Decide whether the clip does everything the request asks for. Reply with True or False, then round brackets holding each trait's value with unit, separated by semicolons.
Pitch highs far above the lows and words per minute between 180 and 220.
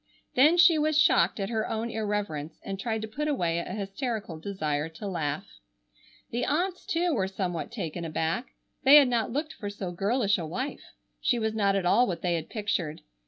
True (6.2 semitones; 195 wpm)